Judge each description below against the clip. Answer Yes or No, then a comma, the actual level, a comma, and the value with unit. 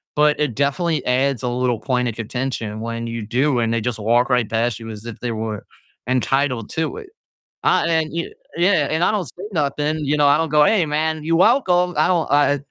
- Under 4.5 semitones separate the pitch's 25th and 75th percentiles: No, average, 5.1 semitones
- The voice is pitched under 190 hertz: Yes, medium, 140 Hz